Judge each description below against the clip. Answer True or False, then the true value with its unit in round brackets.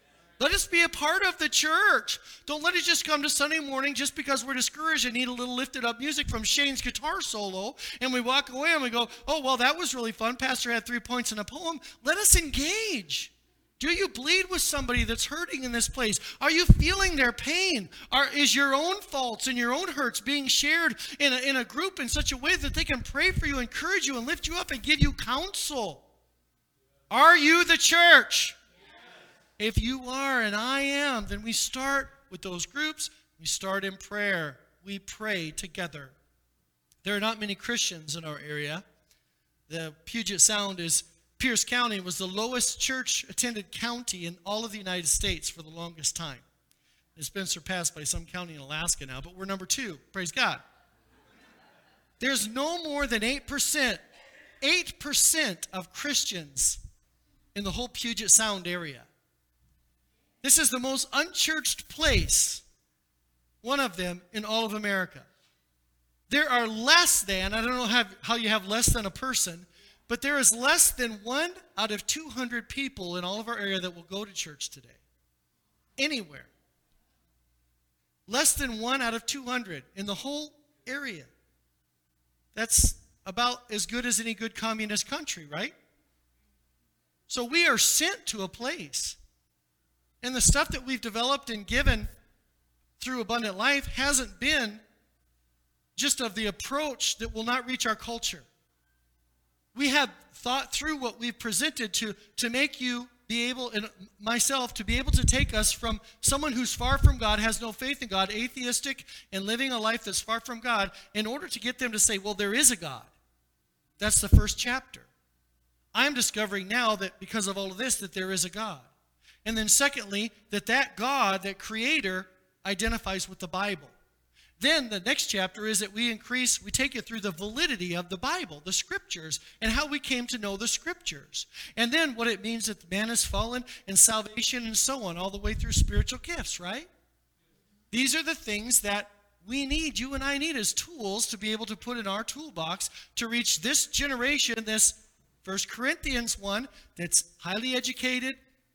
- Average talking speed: True (180 wpm)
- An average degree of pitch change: False (6.4 semitones)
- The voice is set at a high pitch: True (225 Hz)